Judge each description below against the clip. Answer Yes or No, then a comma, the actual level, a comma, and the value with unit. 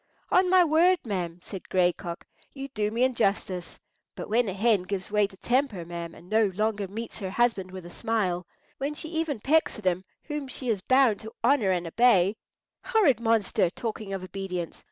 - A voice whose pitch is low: No, high, 210 Hz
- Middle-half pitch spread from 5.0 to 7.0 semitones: Yes, wide, 5.4 semitones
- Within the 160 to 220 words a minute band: Yes, average, 190 wpm